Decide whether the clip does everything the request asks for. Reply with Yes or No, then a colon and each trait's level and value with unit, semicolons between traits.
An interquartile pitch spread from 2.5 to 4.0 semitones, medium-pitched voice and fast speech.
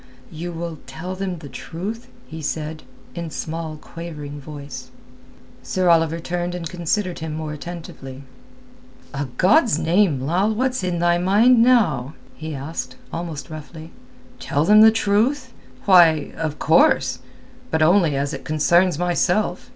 No: average, 3.2 semitones; medium, 170 Hz; slow, 135 wpm